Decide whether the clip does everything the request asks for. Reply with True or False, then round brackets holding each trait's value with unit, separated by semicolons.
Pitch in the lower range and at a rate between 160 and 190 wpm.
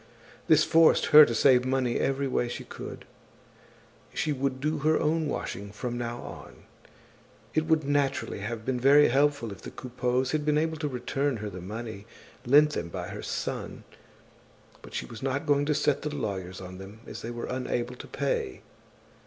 True (130 Hz; 185 wpm)